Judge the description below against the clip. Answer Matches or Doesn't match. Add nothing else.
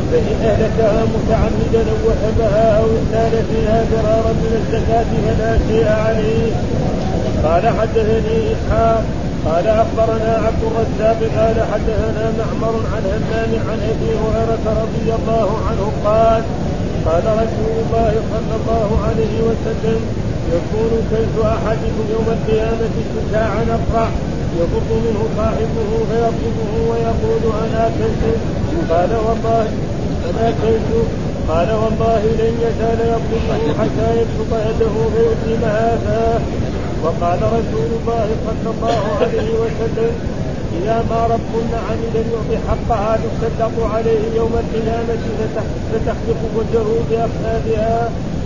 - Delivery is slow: Doesn't match